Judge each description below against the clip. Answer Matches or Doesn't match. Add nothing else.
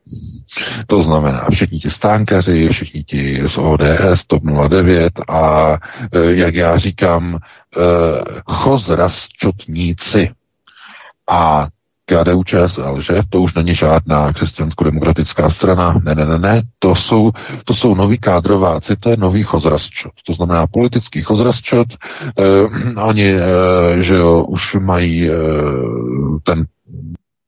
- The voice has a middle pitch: Doesn't match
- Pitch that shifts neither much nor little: Matches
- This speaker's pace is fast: Doesn't match